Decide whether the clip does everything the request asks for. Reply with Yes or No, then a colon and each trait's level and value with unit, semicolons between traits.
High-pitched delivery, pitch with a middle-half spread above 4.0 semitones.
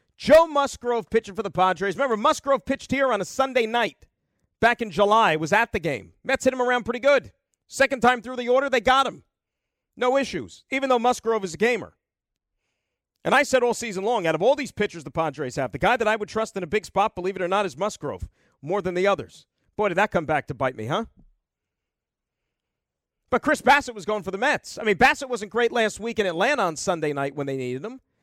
Yes: high, 220 Hz; average, 4.9 semitones